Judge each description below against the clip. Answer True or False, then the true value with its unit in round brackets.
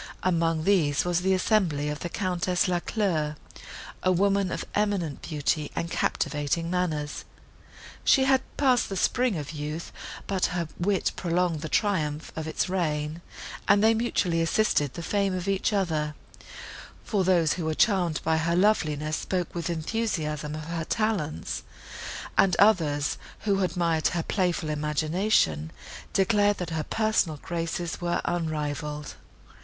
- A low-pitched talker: False (170 Hz)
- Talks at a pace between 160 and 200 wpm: False (140 wpm)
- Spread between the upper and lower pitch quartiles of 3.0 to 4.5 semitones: True (4.0 semitones)